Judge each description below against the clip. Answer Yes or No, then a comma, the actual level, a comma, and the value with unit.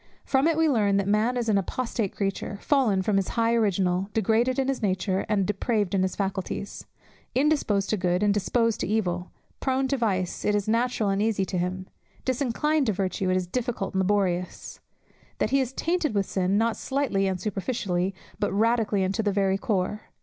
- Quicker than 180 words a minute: Yes, average, 195 wpm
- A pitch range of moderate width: Yes, average, 3.8 semitones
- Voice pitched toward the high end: Yes, high, 205 Hz